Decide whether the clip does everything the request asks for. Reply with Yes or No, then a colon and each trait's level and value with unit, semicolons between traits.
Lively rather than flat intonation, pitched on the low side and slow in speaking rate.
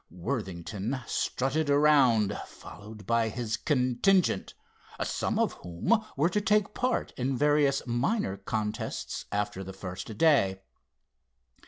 Yes: wide, 6.3 semitones; low, 120 Hz; slow, 115 wpm